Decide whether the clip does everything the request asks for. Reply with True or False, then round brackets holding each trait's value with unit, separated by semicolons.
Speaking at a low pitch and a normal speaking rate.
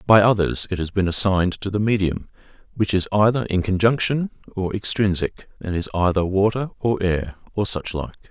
True (100 Hz; 180 wpm)